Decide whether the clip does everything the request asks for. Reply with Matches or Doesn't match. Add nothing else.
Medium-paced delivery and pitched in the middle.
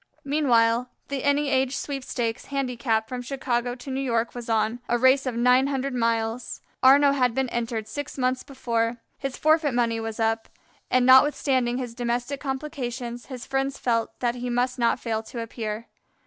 Doesn't match